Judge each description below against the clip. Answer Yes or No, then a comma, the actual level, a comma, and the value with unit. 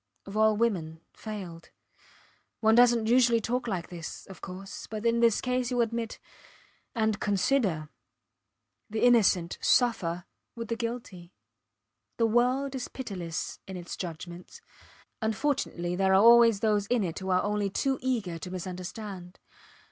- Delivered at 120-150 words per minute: Yes, average, 140 wpm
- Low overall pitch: No, high, 215 Hz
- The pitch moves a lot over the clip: No, average, 4.4 semitones